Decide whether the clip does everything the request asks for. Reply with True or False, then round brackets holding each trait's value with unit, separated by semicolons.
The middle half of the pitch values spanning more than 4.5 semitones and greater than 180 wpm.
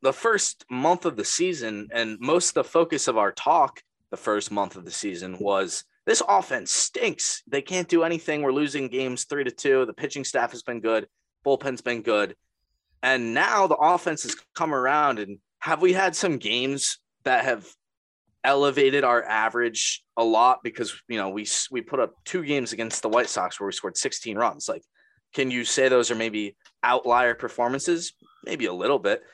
True (5.0 semitones; 190 wpm)